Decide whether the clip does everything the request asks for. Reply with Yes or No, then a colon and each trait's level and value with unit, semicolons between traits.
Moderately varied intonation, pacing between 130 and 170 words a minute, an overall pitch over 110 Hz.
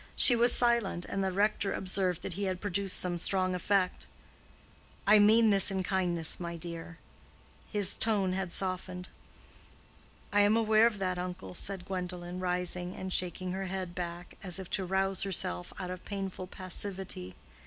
No: narrow, 1.7 semitones; average, 165 wpm; medium, 185 Hz